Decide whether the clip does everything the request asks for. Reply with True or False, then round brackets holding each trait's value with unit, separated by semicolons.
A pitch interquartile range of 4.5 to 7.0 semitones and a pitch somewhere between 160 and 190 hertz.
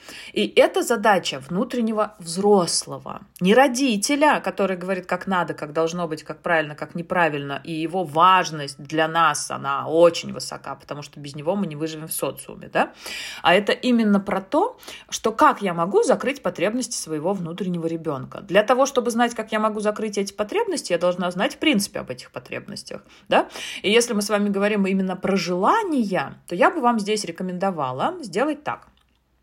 True (4.9 semitones; 185 Hz)